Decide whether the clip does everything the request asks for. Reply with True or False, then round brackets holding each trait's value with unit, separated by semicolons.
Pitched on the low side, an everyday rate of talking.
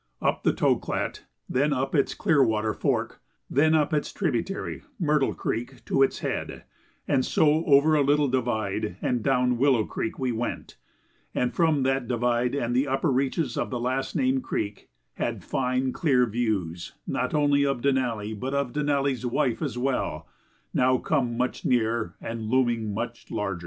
True (130 Hz; 160 wpm)